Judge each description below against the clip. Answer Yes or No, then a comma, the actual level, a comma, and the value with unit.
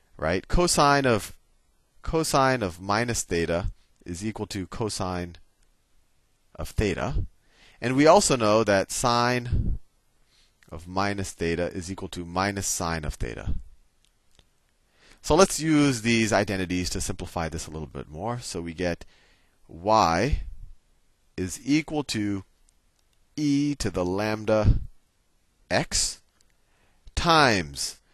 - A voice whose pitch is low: Yes, low, 100 Hz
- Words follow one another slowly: Yes, slow, 115 wpm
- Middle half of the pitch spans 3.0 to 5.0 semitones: No, wide, 5.4 semitones